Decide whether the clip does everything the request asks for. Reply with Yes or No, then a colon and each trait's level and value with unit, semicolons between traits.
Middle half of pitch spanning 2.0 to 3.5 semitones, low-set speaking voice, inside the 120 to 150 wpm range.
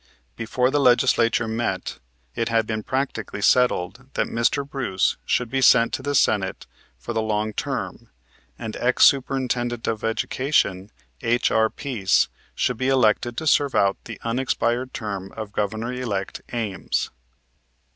Yes: average, 2.9 semitones; low, 115 Hz; average, 140 wpm